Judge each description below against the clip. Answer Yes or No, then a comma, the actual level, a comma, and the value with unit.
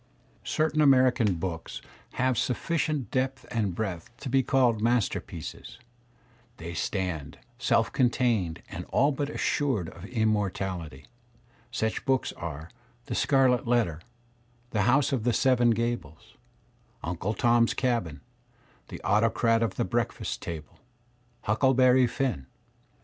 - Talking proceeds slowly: Yes, slow, 120 wpm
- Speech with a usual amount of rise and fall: No, wide, 5.7 semitones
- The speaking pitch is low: Yes, low, 115 Hz